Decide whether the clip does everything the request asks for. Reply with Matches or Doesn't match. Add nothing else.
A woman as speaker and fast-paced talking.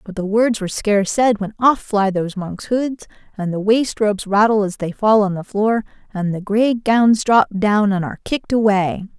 Matches